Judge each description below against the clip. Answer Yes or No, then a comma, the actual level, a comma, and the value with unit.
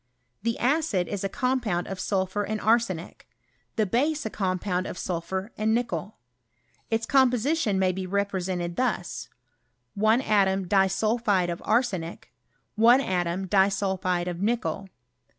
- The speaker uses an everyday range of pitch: Yes, average, 3.7 semitones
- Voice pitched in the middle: No, high, 200 Hz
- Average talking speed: No, slow, 130 wpm